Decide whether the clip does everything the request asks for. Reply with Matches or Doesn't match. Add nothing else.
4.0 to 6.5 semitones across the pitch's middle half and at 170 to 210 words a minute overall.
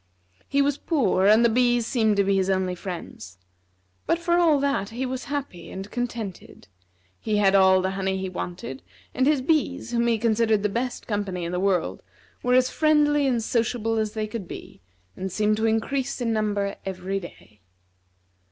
Matches